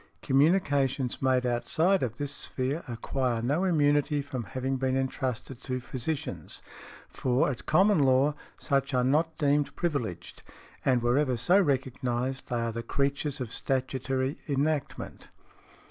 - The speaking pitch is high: No, low, 135 Hz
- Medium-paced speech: No, slow, 130 wpm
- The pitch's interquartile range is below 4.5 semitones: Yes, narrow, 2.4 semitones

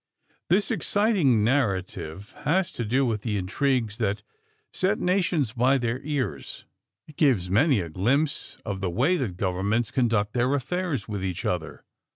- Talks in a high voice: No, low, 120 Hz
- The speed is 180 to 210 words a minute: No, average, 155 wpm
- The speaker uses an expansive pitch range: Yes, wide, 6.4 semitones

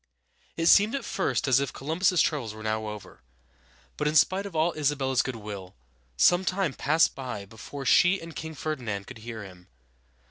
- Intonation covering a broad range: Yes, wide, 7.1 semitones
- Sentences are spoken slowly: No, average, 185 wpm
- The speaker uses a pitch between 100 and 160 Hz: Yes, medium, 140 Hz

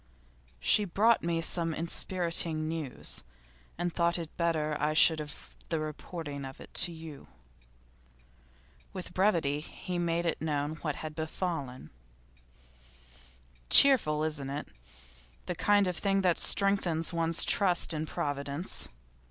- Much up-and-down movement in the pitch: No, narrow, 2.5 semitones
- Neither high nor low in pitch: Yes, medium, 165 Hz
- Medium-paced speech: No, slow, 125 wpm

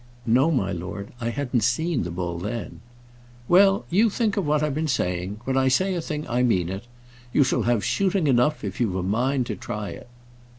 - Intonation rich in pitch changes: Yes, wide, 7.2 semitones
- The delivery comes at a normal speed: No, fast, 215 wpm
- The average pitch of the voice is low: Yes, low, 125 Hz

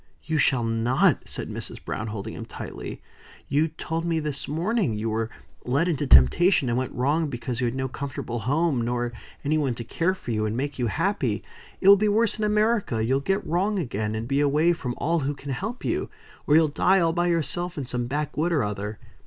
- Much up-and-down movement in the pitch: Yes, wide, 6.0 semitones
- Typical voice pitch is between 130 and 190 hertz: Yes, medium, 140 Hz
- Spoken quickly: Yes, fast, 215 wpm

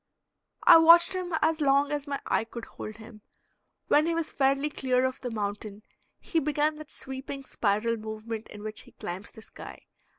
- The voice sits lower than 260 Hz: No, very high, 265 Hz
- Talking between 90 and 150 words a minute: No, average, 185 wpm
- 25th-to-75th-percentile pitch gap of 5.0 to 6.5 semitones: Yes, wide, 5.6 semitones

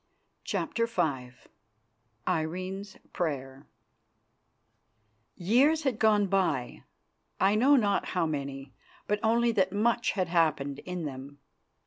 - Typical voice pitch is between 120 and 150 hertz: No, medium, 185 Hz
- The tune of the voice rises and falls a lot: Yes, wide, 7.0 semitones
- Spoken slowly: Yes, slow, 105 wpm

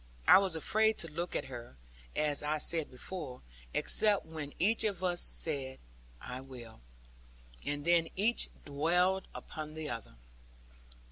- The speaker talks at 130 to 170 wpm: Yes, average, 140 wpm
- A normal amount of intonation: Yes, average, 4.5 semitones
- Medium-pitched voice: Yes, medium, 155 Hz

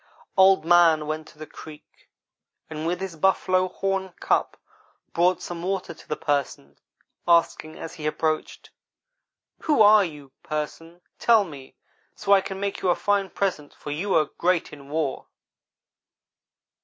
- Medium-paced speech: Yes, average, 150 wpm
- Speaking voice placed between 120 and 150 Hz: No, medium, 170 Hz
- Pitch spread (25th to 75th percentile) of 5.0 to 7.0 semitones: No, average, 3.8 semitones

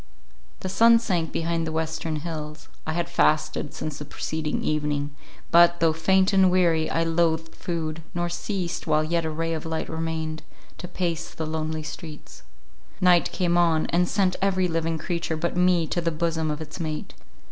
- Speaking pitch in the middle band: Yes, medium, 165 Hz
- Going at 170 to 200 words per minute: Yes, average, 180 wpm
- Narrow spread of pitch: Yes, narrow, 1.6 semitones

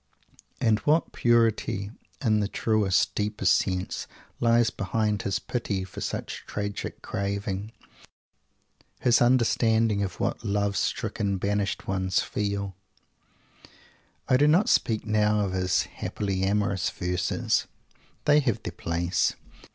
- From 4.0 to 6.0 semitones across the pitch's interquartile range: No, narrow, 2.5 semitones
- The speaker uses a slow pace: Yes, slow, 120 wpm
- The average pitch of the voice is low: Yes, low, 105 Hz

